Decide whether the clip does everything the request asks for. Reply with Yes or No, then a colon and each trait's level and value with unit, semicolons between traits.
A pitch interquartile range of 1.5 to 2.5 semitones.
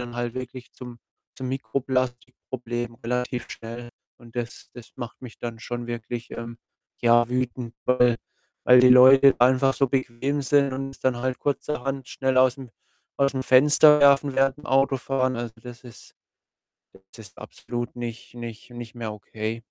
Yes: narrow, 1.9 semitones